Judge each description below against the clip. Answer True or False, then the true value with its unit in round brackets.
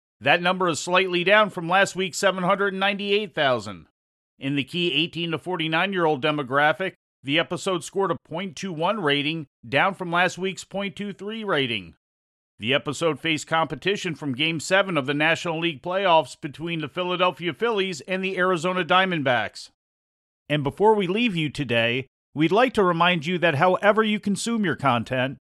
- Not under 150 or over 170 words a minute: True (155 wpm)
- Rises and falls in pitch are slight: False (4.4 semitones)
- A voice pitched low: False (170 Hz)